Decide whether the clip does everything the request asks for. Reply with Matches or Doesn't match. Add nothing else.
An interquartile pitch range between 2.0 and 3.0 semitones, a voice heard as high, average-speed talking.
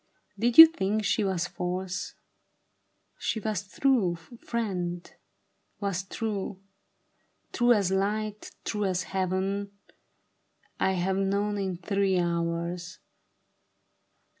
Doesn't match